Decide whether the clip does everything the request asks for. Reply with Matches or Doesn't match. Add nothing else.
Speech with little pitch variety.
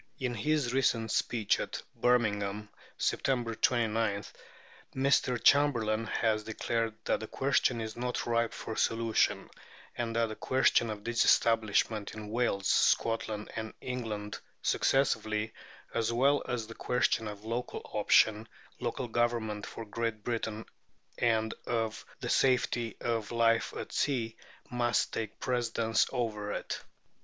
Matches